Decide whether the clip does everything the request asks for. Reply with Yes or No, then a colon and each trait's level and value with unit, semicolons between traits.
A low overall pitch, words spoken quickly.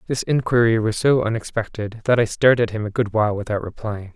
Yes: low, 110 Hz; fast, 215 wpm